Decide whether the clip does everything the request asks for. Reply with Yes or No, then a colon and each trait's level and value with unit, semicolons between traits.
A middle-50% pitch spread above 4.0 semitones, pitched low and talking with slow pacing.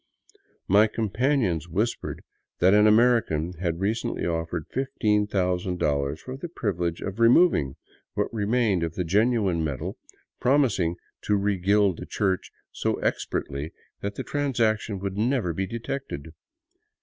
Yes: average, 5.0 semitones; low, 100 Hz; slow, 125 wpm